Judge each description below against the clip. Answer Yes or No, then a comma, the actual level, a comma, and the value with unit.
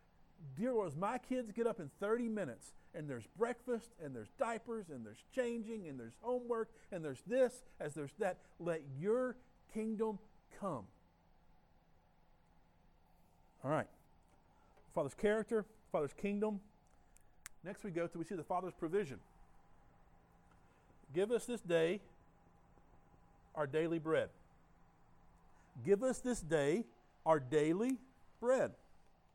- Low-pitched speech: No, high, 190 Hz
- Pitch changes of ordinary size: No, wide, 7.7 semitones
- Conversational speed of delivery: No, slow, 125 wpm